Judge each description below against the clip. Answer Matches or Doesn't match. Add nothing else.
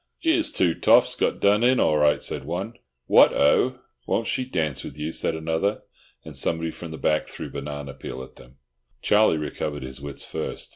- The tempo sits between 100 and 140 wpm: Doesn't match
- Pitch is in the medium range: Doesn't match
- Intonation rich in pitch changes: Matches